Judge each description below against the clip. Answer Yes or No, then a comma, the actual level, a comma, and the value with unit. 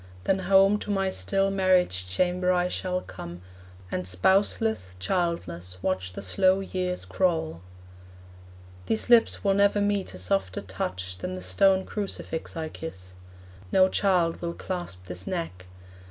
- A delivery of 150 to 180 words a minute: No, average, 140 wpm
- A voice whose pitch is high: No, medium, 180 Hz